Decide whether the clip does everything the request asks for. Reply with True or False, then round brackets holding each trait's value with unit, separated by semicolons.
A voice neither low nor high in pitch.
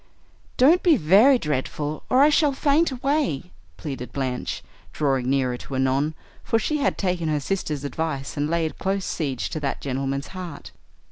True (155 Hz)